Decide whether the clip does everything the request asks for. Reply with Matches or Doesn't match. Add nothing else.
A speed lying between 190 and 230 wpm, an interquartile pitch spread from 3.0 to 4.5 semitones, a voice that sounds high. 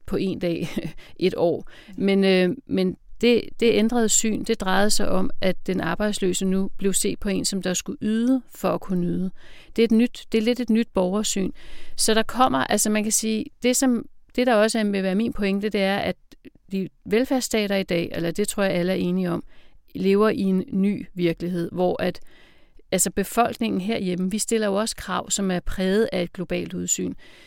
Matches